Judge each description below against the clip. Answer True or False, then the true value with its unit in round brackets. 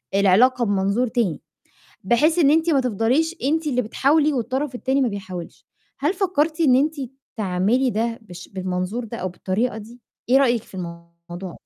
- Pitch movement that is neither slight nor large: False (6.3 semitones)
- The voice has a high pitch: True (240 Hz)